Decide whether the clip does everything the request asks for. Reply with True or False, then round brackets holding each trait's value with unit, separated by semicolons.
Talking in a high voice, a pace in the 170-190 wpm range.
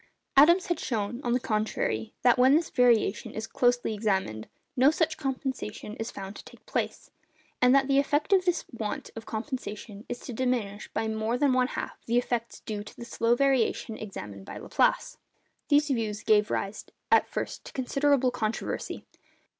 True (240 Hz; 175 wpm)